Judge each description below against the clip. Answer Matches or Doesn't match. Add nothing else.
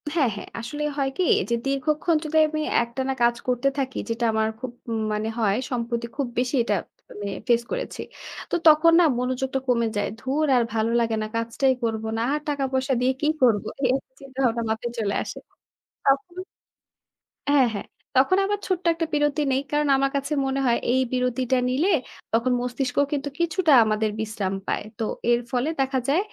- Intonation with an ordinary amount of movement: Matches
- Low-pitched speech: Doesn't match